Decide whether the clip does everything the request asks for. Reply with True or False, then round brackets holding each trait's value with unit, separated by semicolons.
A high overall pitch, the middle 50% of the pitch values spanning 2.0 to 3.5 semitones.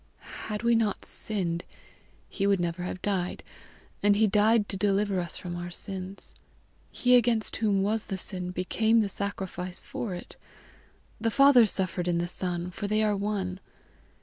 True (200 Hz; 2.9 semitones)